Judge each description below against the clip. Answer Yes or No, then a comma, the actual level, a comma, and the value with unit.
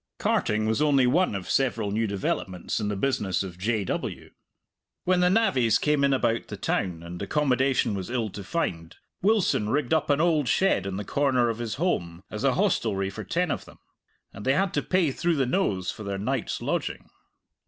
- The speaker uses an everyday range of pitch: No, wide, 6.9 semitones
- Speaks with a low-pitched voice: Yes, low, 120 Hz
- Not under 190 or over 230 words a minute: Yes, average, 200 wpm